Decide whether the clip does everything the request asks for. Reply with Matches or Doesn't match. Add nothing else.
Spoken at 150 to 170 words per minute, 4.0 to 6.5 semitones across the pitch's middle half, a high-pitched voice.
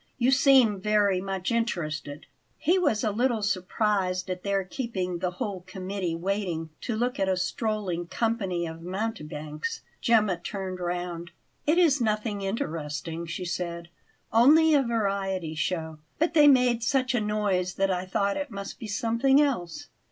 Matches